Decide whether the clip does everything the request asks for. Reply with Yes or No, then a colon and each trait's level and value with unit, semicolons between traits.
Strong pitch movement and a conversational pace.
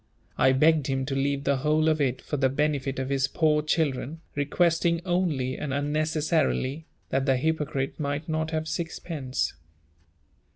No: average, 2.8 semitones; average, 155 wpm